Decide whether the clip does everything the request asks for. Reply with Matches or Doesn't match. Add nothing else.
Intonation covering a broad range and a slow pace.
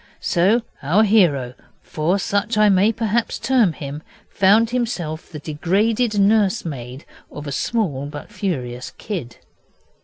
Matches